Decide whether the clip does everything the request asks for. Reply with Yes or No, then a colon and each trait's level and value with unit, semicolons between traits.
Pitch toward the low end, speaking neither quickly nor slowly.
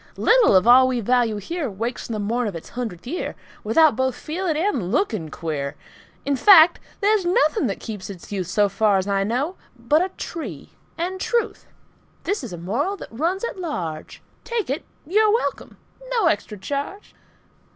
No: very high, 250 Hz; average, 180 wpm